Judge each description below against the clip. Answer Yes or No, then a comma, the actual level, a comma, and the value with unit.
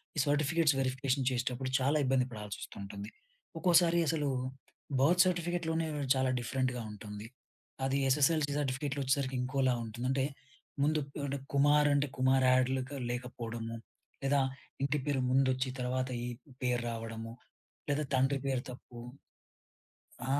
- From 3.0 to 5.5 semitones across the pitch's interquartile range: No, narrow, 2.5 semitones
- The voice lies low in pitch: Yes, low, 130 Hz